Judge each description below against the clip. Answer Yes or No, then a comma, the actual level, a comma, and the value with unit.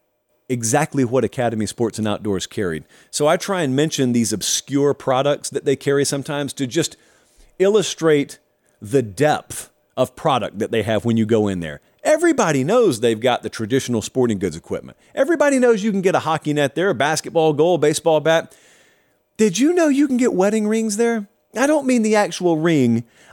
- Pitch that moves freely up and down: Yes, wide, 8.6 semitones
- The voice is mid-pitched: Yes, medium, 145 Hz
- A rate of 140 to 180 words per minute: No, average, 190 wpm